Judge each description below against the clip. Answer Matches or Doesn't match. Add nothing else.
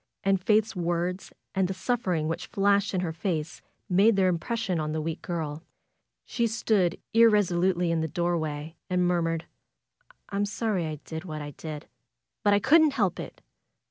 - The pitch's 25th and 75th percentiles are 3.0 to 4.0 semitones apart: Matches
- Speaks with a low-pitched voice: Doesn't match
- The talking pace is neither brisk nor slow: Matches